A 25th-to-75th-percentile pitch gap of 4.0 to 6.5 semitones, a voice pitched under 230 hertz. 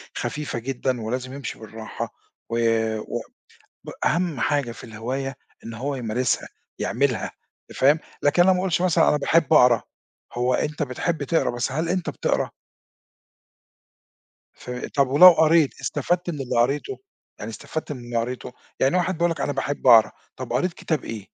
Yes: average, 5.1 semitones; medium, 140 Hz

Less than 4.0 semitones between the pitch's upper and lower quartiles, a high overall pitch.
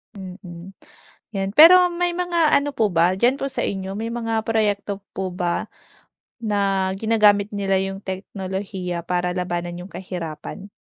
Yes: average, 3.6 semitones; high, 195 Hz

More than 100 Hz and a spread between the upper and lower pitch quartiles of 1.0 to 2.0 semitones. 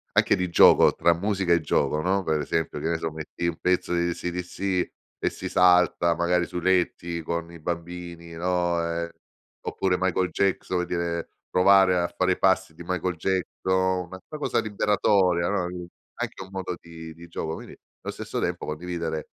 No: very low, 90 Hz; narrow, 1.6 semitones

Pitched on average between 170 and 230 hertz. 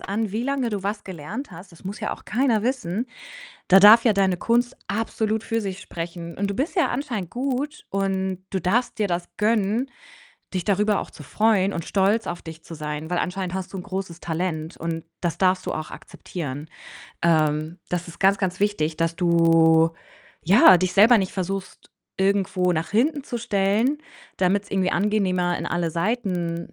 Yes: high, 190 Hz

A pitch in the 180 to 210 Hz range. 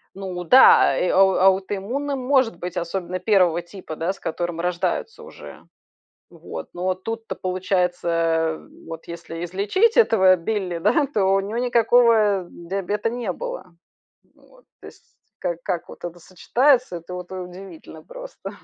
Yes: medium, 185 Hz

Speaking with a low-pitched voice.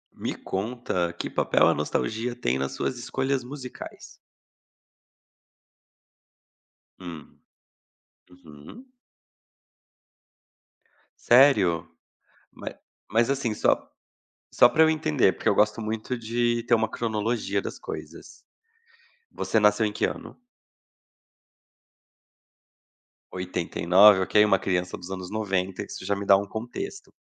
Yes: low, 105 Hz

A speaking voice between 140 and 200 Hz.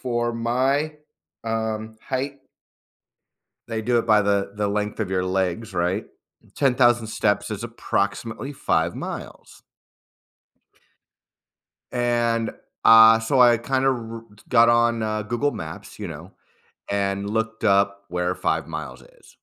No: low, 110 Hz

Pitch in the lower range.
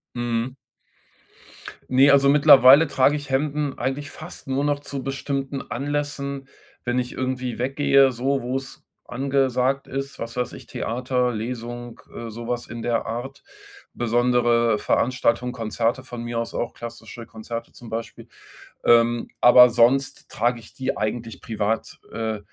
Yes: low, 125 Hz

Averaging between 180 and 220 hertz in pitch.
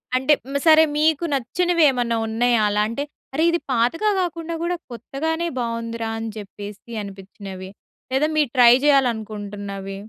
No: high, 240 Hz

